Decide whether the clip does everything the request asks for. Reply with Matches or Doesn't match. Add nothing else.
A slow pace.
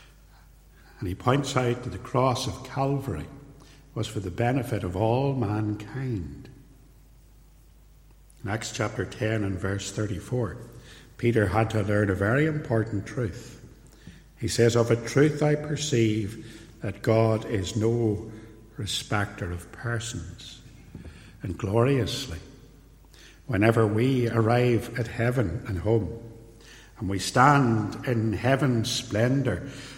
Matches